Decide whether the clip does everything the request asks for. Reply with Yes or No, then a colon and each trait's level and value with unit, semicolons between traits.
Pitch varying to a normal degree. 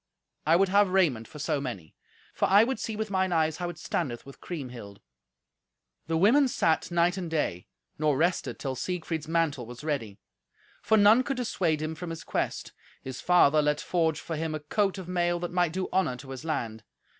Yes: average, 4.1 semitones